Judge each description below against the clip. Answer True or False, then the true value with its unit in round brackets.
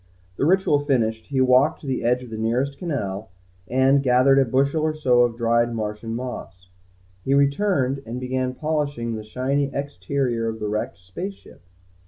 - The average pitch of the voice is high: False (130 Hz)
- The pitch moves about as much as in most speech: True (3.5 semitones)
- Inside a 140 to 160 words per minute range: False (175 wpm)